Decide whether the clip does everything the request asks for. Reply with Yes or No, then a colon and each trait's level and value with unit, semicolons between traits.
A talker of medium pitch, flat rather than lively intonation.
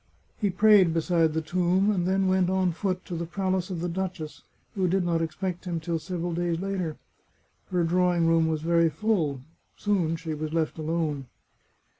Yes: medium, 175 Hz; narrow, 2.3 semitones